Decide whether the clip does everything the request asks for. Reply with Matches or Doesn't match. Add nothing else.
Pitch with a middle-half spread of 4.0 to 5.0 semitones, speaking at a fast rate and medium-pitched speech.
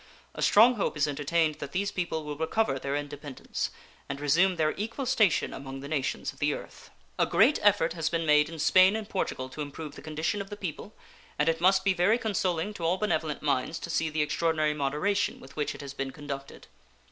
Matches